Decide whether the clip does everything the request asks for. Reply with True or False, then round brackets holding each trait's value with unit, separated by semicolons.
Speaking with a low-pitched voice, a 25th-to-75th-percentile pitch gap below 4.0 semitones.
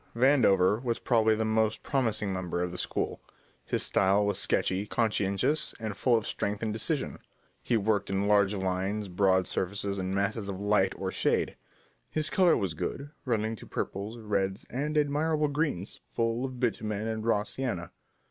True (105 Hz; 3.5 semitones)